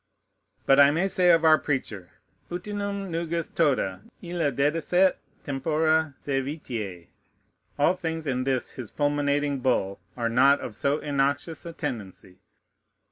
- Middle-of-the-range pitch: Yes, medium, 145 Hz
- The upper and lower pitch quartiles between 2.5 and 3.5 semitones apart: No, average, 4.2 semitones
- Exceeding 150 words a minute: No, slow, 135 wpm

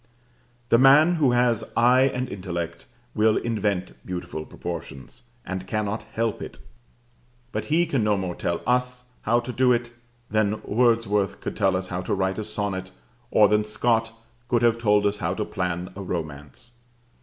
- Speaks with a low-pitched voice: Yes, low, 105 Hz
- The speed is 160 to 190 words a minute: Yes, average, 165 wpm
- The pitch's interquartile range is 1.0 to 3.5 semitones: No, average, 4.2 semitones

